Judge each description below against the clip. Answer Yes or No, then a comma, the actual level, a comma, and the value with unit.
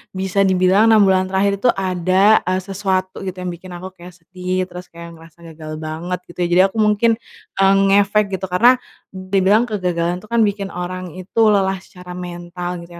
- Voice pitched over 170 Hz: Yes, medium, 185 Hz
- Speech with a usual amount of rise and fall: No, narrow, 1.8 semitones